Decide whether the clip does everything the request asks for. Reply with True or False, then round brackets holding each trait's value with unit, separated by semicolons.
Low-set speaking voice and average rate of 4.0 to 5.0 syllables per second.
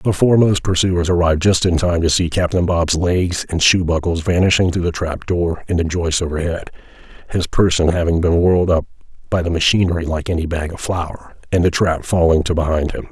False (85 Hz; 5.5 syllables/s)